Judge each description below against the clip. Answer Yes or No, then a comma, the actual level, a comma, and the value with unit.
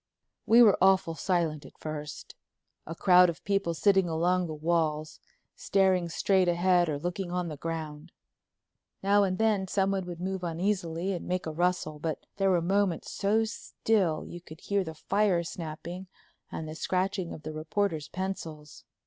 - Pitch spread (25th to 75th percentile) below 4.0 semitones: Yes, average, 3.2 semitones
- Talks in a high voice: No, medium, 175 Hz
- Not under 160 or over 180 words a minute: Yes, average, 165 wpm